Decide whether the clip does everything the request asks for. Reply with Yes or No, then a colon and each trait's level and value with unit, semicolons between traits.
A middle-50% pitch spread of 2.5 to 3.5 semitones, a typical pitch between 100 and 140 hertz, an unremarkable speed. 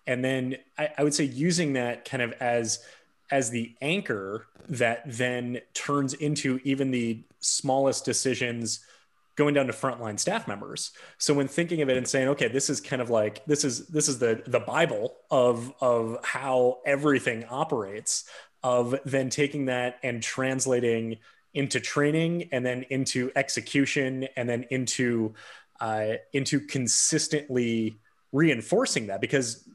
Yes: average, 2.8 semitones; low, 130 Hz; average, 150 wpm